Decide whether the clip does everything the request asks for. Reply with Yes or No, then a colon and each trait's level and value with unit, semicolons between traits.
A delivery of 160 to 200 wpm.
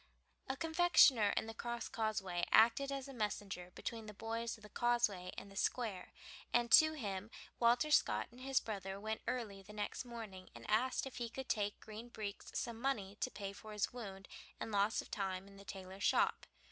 Yes: average, 190 wpm